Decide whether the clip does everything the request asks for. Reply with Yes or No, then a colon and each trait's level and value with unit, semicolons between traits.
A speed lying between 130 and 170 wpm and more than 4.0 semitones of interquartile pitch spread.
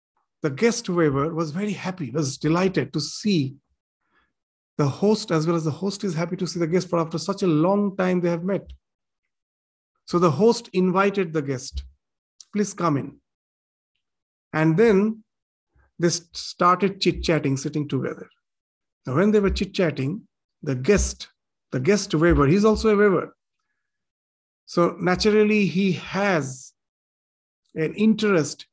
Yes: average, 145 wpm; average, 5.2 semitones